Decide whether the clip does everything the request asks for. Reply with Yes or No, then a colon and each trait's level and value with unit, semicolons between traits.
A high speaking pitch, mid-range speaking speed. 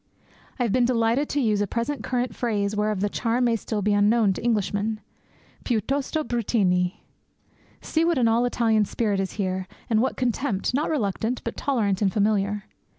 Yes: high, 225 Hz; average, 175 wpm